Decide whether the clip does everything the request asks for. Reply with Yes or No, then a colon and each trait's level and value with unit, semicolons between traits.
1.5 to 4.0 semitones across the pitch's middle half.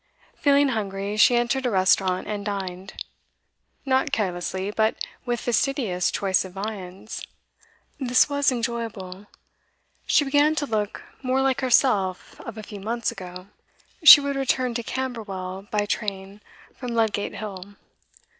No: average, 4.8 semitones